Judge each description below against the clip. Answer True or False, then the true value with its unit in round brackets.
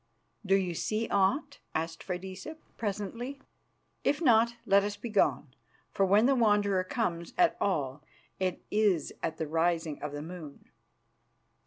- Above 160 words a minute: False (145 wpm)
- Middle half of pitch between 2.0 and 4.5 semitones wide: False (5.0 semitones)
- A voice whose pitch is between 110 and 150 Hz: False (195 Hz)